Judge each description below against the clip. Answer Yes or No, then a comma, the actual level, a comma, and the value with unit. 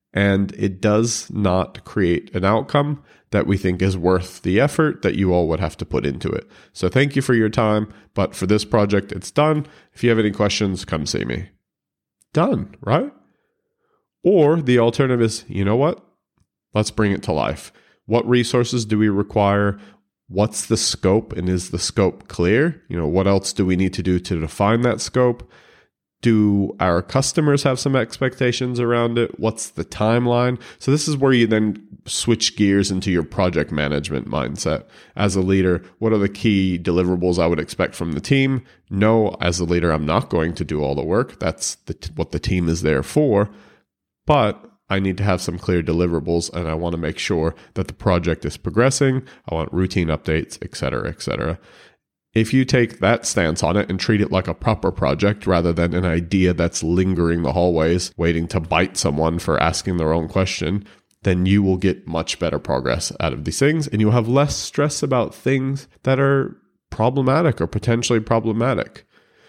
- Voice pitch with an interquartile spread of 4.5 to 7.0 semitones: Yes, average, 5.0 semitones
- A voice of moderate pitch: No, low, 100 Hz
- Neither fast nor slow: Yes, average, 195 wpm